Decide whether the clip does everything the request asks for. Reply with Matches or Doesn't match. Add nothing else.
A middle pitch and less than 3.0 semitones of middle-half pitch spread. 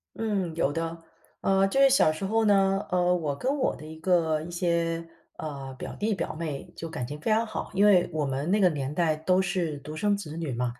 Doesn't match